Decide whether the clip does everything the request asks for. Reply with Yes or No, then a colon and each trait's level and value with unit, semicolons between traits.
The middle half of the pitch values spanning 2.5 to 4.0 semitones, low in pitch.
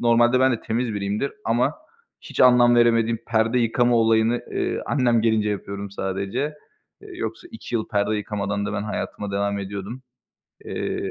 Yes: average, 2.9 semitones; low, 115 Hz